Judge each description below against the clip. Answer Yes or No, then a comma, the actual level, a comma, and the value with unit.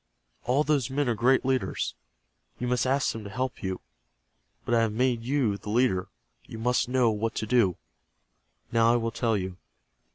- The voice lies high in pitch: No, low, 120 Hz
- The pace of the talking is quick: No, average, 185 wpm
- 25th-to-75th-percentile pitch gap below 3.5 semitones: Yes, average, 2.7 semitones